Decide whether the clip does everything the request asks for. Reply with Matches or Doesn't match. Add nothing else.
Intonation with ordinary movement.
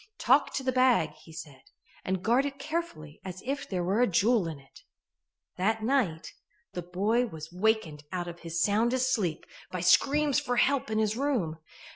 Doesn't match